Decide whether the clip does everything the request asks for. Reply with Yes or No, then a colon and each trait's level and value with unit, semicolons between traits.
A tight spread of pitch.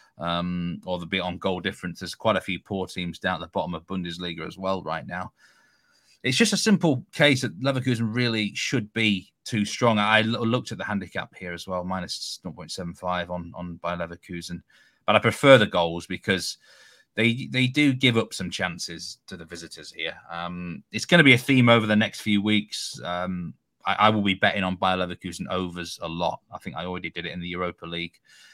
No: average, 4.5 semitones